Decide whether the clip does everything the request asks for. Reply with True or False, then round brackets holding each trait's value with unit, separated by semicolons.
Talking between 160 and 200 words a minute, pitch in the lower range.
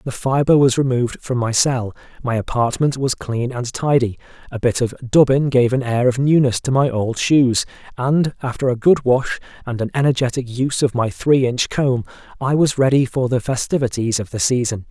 True (195 wpm; 125 Hz)